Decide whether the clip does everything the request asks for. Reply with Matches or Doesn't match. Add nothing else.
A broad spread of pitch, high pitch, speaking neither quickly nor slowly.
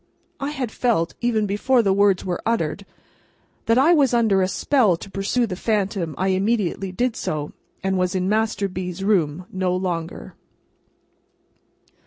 Doesn't match